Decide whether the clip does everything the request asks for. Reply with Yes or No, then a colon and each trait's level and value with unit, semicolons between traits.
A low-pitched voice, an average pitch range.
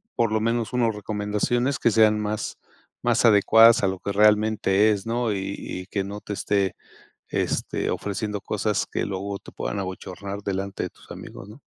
No: low, 105 Hz; narrow, 1.9 semitones